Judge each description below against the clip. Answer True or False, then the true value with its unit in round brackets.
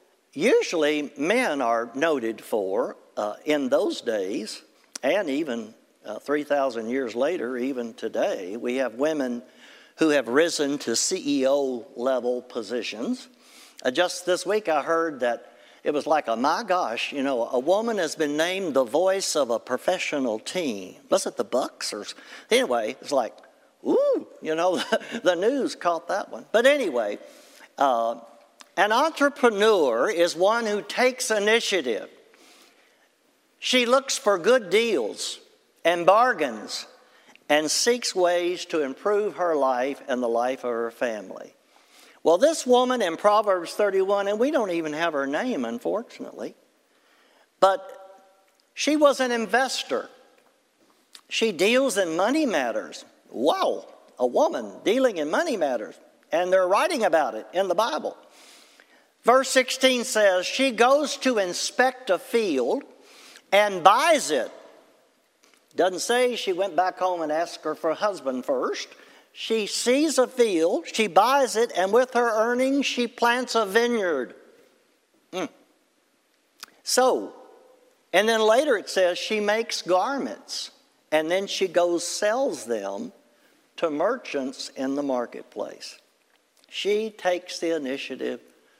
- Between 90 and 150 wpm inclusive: True (140 wpm)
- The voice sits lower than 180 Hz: False (195 Hz)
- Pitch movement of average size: False (8.5 semitones)